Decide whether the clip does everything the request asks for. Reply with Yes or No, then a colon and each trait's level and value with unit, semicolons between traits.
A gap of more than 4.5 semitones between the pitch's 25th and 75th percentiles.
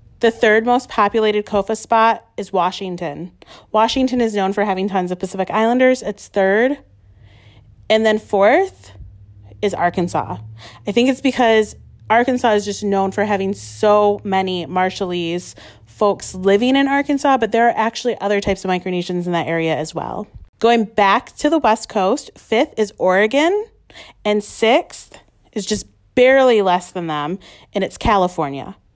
No: average, 4.2 semitones